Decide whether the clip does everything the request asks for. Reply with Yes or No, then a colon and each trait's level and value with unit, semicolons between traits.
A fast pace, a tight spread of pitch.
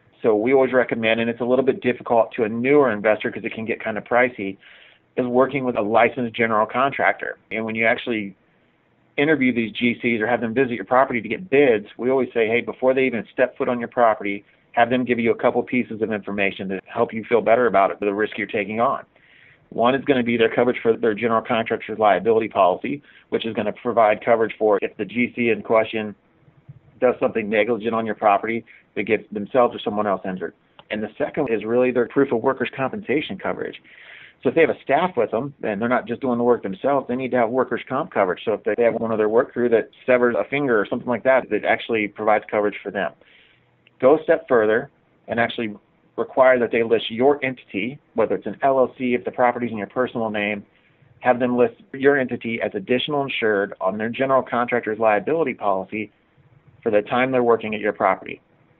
Yes: fast, 220 wpm; narrow, 2.3 semitones